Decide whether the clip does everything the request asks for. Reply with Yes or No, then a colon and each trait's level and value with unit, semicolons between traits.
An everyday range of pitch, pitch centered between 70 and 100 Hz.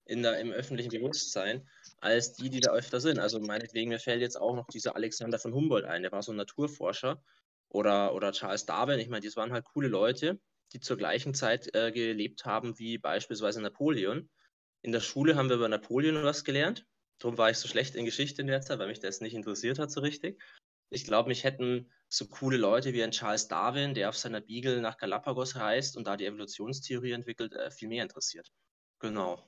No: average, 3.2 semitones; low, 120 Hz